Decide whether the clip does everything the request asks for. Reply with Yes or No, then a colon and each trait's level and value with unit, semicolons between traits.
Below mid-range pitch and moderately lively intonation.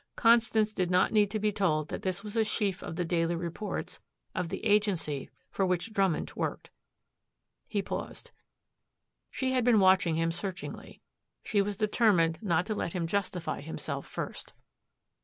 No: high, 195 Hz; average, 3.7 semitones